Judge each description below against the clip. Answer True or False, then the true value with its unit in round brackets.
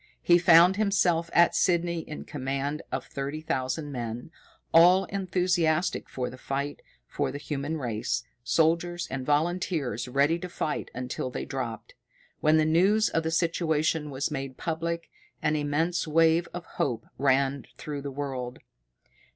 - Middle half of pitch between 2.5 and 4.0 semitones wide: True (3.7 semitones)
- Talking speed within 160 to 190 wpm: False (145 wpm)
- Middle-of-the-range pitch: True (155 Hz)